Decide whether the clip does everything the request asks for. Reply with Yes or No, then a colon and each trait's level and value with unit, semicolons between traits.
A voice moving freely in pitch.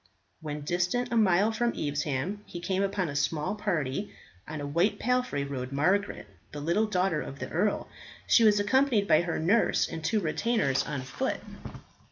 Yes: wide, 6.1 semitones